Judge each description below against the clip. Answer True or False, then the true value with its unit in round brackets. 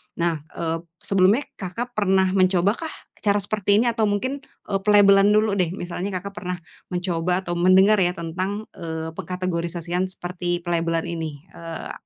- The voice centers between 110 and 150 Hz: False (185 Hz)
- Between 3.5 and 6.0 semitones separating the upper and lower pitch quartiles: False (2.8 semitones)